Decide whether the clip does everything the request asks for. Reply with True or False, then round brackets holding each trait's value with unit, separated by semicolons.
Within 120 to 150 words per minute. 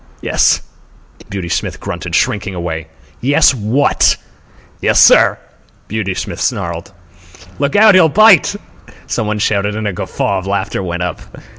True (140 wpm)